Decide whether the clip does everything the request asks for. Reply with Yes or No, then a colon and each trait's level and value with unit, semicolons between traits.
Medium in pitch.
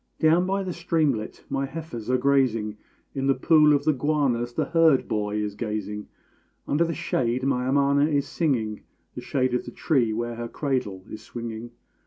No: low, 130 Hz